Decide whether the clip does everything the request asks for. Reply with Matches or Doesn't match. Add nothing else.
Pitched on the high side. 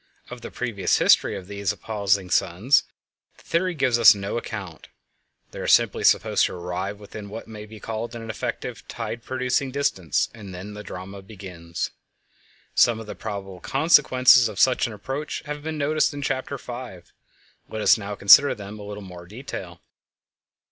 Doesn't match